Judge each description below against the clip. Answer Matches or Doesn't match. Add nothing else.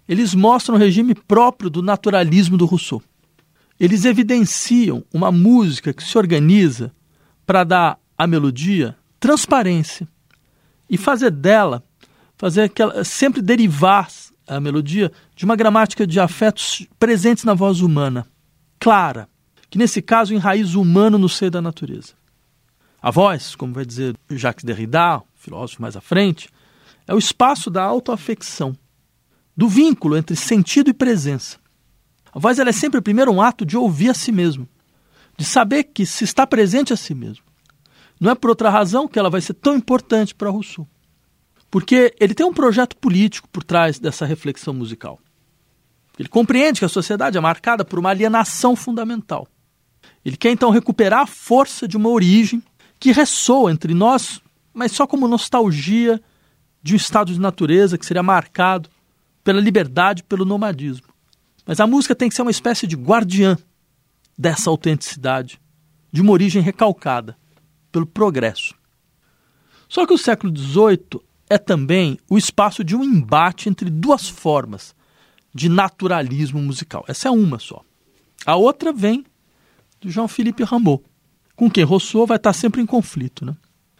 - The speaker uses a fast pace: Doesn't match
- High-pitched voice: Matches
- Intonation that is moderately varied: Doesn't match